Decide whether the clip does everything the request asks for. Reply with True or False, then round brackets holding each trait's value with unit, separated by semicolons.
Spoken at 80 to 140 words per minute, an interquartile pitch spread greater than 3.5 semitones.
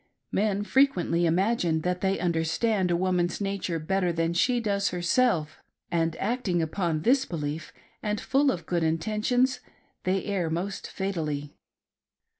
True (135 wpm; 3.9 semitones)